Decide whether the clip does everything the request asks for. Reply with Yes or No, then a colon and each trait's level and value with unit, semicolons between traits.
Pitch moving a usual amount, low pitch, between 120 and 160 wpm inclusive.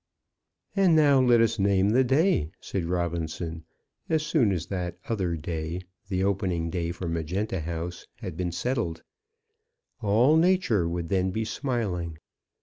No: wide, 5.7 semitones; very low, 95 Hz; average, 145 wpm